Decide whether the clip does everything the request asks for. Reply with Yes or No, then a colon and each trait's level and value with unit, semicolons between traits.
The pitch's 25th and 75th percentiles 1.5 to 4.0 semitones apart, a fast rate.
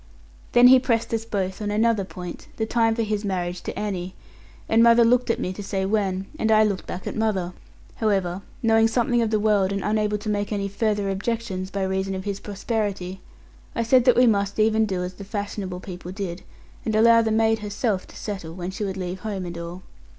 Yes: average, 2.8 semitones; fast, 215 wpm